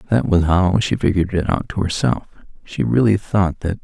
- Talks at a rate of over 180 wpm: Yes, fast, 205 wpm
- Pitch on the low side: Yes, very low, 95 Hz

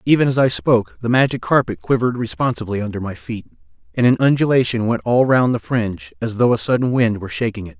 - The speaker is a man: Yes, male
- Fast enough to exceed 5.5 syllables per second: Yes, 6.5 syllables/s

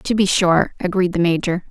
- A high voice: No, medium, 180 Hz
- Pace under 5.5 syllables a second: Yes, 5.0 syllables/s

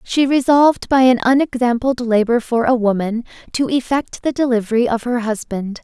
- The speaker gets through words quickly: No, average, 165 wpm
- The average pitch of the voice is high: Yes, high, 245 Hz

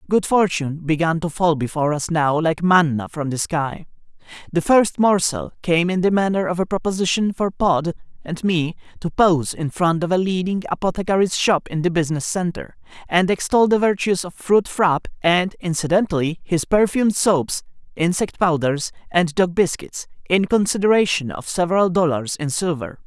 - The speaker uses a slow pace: No, average, 165 wpm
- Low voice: No, medium, 175 Hz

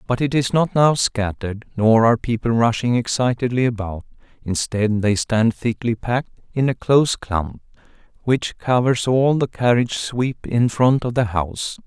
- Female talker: No, male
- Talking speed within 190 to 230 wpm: No, average, 160 wpm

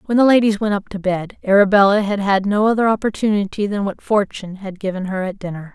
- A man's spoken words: No, female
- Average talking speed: No, fast, 220 wpm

